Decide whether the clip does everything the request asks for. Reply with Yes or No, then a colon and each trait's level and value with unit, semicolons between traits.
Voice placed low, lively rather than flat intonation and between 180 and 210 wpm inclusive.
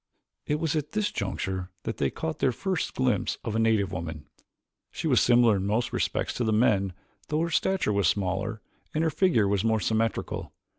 Yes: low, 115 Hz; wide, 7.2 semitones; average, 190 wpm